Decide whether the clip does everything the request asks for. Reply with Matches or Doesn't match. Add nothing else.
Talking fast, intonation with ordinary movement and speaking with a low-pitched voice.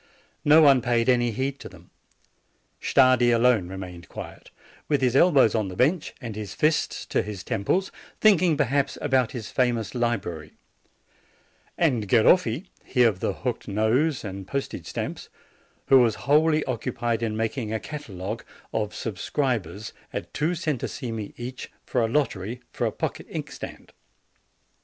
Doesn't match